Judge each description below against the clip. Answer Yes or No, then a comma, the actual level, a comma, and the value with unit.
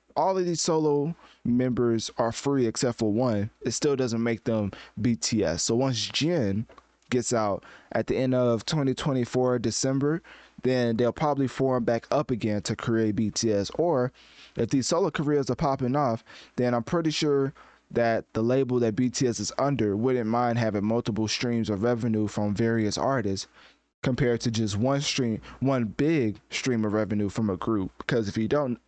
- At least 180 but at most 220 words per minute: No, average, 170 wpm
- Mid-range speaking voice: No, low, 120 Hz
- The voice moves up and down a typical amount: Yes, average, 3.3 semitones